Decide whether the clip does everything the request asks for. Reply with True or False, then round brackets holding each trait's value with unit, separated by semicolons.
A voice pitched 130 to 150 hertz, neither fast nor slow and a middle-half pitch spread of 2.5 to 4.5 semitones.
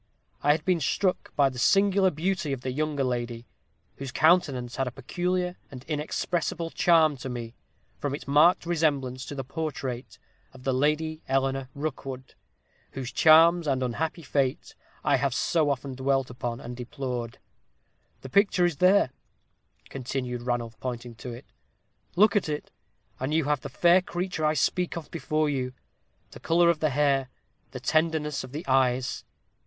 True (140 Hz; 160 wpm; 4.0 semitones)